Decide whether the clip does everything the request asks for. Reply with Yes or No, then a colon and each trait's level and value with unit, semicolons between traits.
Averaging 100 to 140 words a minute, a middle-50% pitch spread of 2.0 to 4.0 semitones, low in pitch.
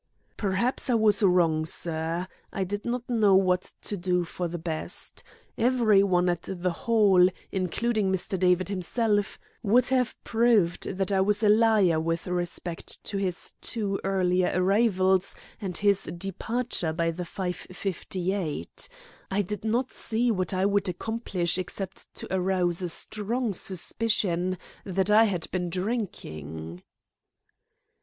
No: slow, 135 wpm; average, 3.0 semitones; high, 190 Hz